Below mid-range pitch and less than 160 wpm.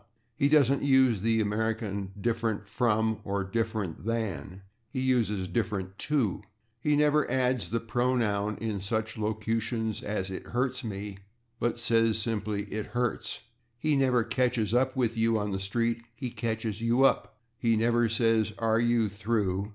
Yes: low, 115 Hz; average, 150 wpm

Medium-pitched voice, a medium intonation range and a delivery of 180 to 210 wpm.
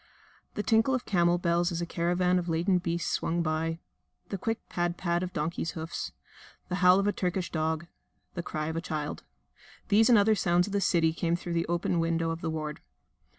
No: medium, 175 Hz; narrow, 1.8 semitones; fast, 205 wpm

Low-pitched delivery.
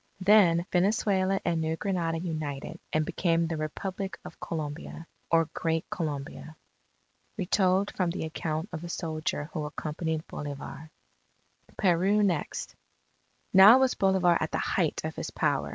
No: medium, 165 Hz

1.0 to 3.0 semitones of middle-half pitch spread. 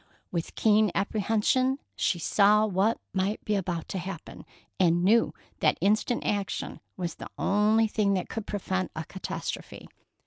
Yes: narrow, 2.5 semitones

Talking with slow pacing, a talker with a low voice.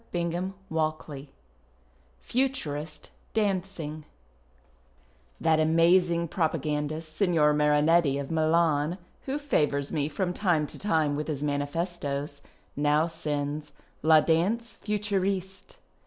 No: slow, 100 wpm; medium, 160 Hz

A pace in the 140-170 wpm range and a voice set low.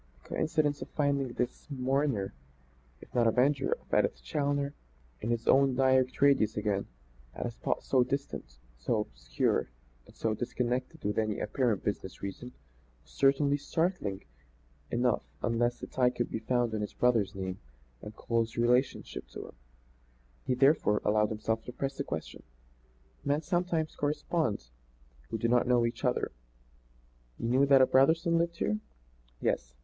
Yes: average, 155 wpm; low, 125 Hz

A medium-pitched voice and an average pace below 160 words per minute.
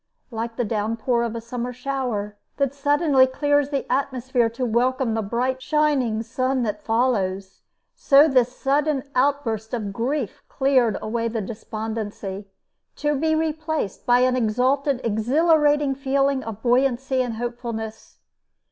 No: very high, 250 Hz; slow, 135 wpm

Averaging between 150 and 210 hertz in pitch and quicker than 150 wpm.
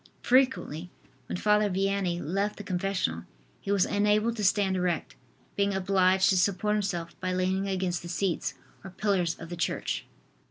Yes: high, 190 Hz; average, 160 wpm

